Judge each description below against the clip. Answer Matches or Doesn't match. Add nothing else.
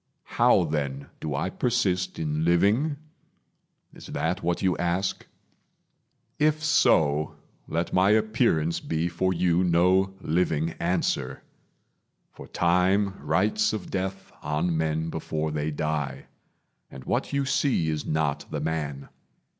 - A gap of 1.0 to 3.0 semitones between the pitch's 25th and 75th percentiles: Doesn't match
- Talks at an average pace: Doesn't match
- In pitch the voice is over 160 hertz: Doesn't match